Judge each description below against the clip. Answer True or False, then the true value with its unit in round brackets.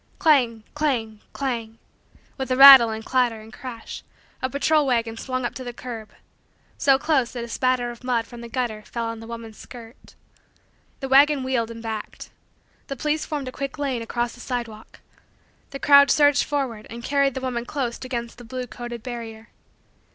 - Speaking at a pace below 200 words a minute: True (180 wpm)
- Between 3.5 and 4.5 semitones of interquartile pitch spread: False (2.7 semitones)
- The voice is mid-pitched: False (245 Hz)